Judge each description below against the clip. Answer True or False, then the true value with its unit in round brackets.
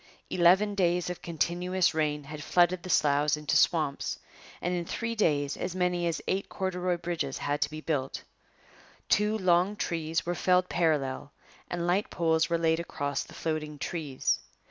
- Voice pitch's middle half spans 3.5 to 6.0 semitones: False (3.0 semitones)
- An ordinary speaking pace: True (165 wpm)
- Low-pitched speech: False (170 Hz)